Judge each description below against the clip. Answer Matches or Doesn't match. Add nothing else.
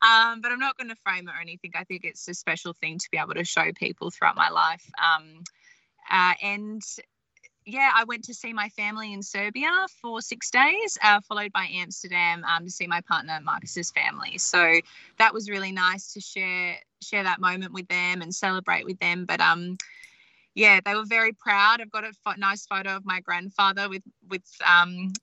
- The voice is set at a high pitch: Matches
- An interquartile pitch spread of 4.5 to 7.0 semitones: Doesn't match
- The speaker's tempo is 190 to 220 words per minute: Matches